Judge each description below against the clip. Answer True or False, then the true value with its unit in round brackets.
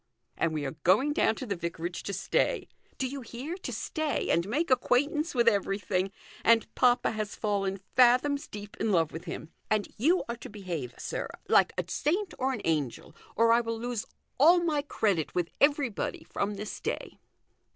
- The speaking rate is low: False (180 wpm)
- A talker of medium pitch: False (225 Hz)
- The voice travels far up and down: True (6.0 semitones)